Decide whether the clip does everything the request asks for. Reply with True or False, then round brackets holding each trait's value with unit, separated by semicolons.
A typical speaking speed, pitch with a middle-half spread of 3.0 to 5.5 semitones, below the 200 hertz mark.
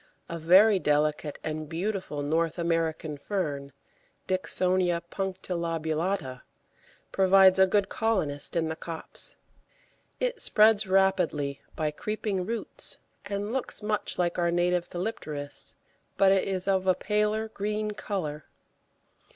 False (115 wpm; 4.0 semitones; 185 Hz)